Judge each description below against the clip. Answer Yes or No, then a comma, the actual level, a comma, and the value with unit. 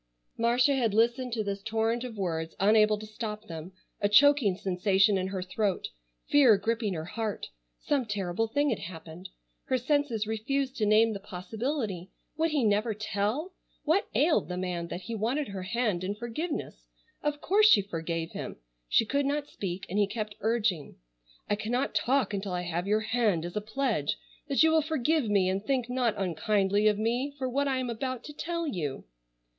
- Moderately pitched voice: No, high, 215 Hz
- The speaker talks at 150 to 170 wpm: No, average, 185 wpm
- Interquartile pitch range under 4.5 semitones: No, average, 4.9 semitones